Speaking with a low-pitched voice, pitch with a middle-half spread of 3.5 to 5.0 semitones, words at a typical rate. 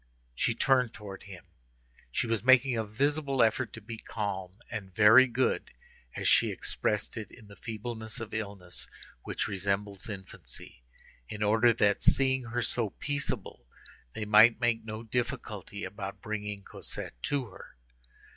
No: low, 110 Hz; average, 3.1 semitones; average, 145 wpm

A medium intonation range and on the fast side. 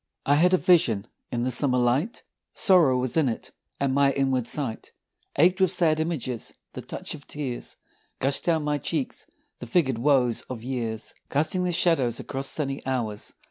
No: average, 4.2 semitones; average, 175 wpm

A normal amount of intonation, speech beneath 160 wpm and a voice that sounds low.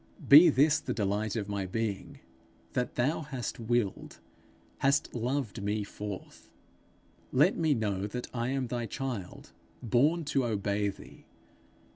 Yes: average, 4.9 semitones; slow, 135 wpm; low, 120 Hz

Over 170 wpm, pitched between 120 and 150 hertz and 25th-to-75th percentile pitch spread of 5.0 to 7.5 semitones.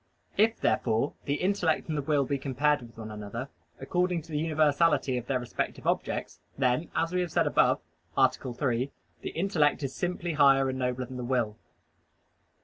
No: average, 180 wpm; medium, 140 Hz; average, 4.3 semitones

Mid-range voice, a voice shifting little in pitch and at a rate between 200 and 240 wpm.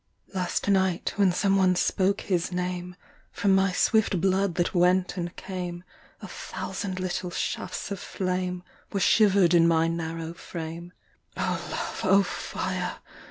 No: medium, 180 Hz; narrow, 1.7 semitones; average, 145 wpm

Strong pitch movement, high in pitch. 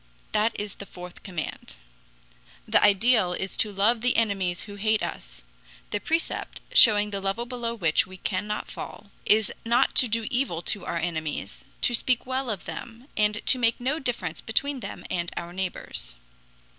No: average, 4.2 semitones; high, 210 Hz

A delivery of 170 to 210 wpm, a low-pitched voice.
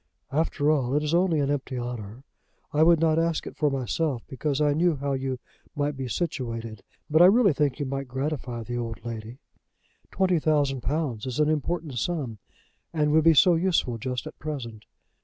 No: average, 190 wpm; medium, 145 Hz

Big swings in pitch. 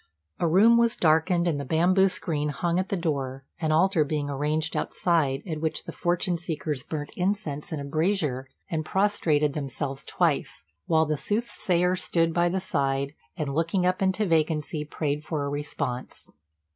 No: average, 3.5 semitones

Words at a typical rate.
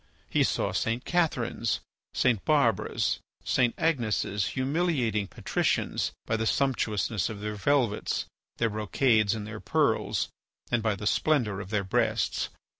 No: slow, 130 wpm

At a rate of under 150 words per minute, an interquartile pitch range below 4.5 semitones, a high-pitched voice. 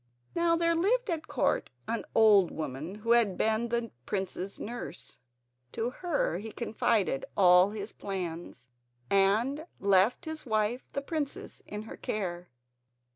No: slow, 135 wpm; average, 5.0 semitones; high, 215 Hz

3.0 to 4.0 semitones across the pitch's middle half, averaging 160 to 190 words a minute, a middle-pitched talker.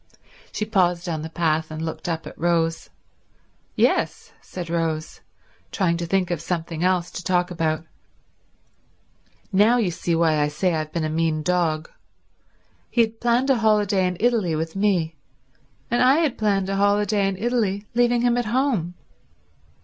No: average, 4.5 semitones; average, 165 wpm; medium, 180 Hz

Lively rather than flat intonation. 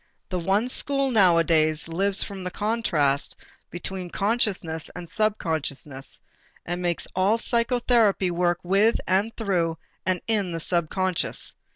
No: average, 4.2 semitones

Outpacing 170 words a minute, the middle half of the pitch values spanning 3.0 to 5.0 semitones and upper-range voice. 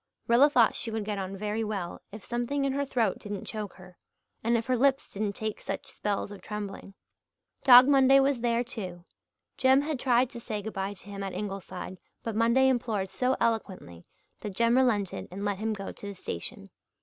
Yes: average, 200 wpm; average, 3.9 semitones; high, 220 Hz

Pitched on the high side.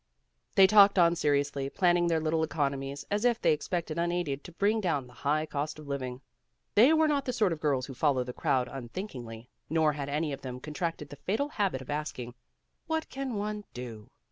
No: medium, 155 Hz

